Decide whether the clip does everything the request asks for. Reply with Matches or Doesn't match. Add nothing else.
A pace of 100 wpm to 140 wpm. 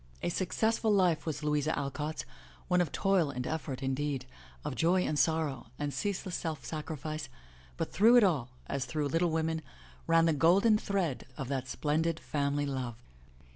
Doesn't match